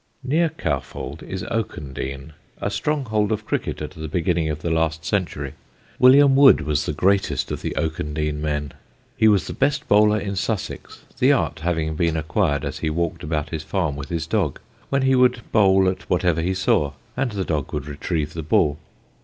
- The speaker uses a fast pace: No, average, 185 wpm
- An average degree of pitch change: No, wide, 5.7 semitones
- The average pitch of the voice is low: Yes, very low, 85 Hz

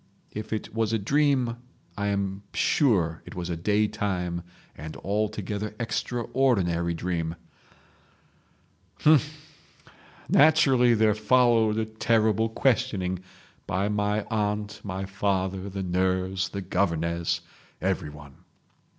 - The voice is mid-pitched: No, low, 105 Hz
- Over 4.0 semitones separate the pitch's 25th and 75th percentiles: No, average, 3.5 semitones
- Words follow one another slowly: Yes, slow, 100 wpm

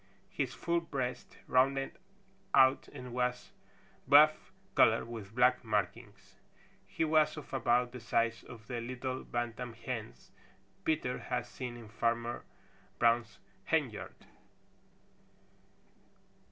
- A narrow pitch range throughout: Yes, narrow, 2.0 semitones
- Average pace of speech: No, slow, 110 wpm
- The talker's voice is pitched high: No, low, 125 Hz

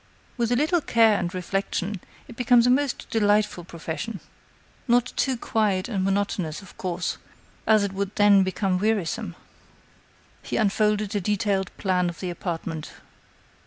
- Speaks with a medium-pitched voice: No, high, 200 Hz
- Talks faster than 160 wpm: No, average, 145 wpm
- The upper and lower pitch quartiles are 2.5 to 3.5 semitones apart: Yes, average, 3.2 semitones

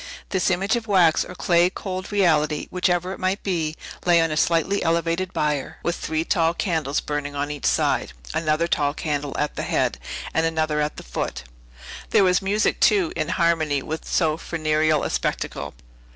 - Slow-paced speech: No, average, 180 wpm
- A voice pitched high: No, medium, 165 Hz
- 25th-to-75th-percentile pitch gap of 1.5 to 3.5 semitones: Yes, average, 3.1 semitones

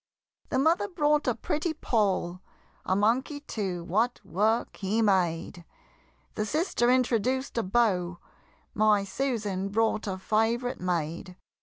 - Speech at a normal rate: No, slow, 125 wpm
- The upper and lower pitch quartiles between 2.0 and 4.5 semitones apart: No, average, 5.1 semitones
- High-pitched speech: Yes, high, 215 Hz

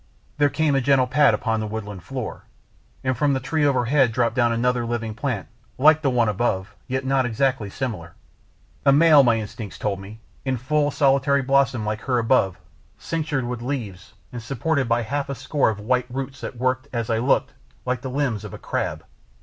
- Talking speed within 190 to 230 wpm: Yes, average, 200 wpm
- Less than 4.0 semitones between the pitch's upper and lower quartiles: Yes, average, 3.4 semitones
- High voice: No, low, 125 Hz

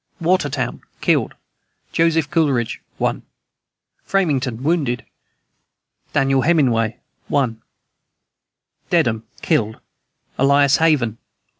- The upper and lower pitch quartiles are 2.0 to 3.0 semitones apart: No, average, 5.1 semitones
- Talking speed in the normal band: No, slow, 80 wpm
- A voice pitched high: No, medium, 140 Hz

